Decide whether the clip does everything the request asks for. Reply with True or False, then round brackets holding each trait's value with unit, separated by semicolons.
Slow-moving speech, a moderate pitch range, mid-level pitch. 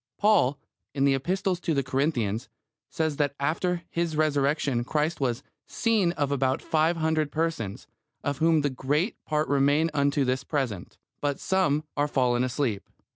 False (155 wpm; 3.0 semitones; 145 Hz)